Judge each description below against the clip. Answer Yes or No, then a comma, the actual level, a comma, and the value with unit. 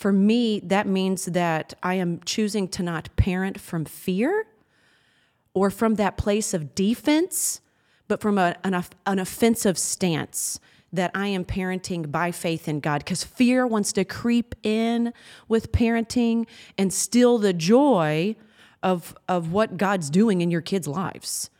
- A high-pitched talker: Yes, high, 195 Hz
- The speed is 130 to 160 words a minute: Yes, average, 155 wpm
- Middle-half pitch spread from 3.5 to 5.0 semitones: Yes, average, 3.8 semitones